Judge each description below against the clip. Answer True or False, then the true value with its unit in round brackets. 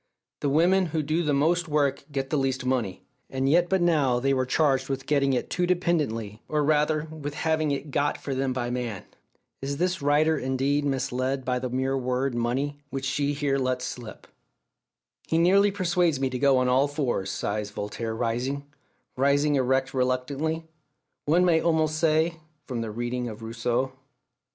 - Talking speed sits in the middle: True (175 wpm)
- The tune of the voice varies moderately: True (3.4 semitones)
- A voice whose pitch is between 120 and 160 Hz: True (140 Hz)